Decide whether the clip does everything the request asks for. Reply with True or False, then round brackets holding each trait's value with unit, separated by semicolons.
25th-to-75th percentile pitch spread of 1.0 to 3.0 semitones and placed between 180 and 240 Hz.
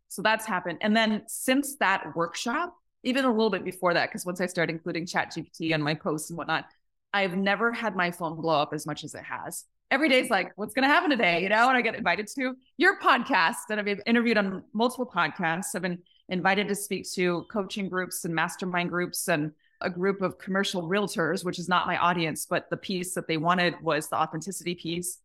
False (4.3 semitones; 185 Hz)